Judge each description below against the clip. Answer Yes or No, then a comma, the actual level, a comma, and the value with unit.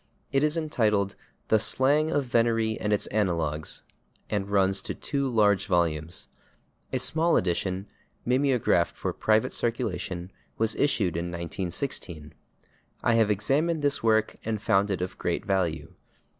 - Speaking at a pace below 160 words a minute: Yes, average, 140 wpm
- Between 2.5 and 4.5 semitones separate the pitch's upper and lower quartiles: No, average, 5.3 semitones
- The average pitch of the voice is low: Yes, low, 105 Hz